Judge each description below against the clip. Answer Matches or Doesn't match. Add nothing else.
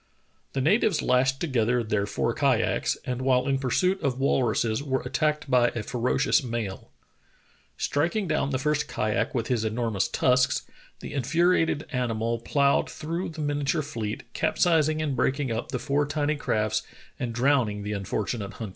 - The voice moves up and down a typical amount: Matches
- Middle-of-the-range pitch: Doesn't match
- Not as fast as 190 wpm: Matches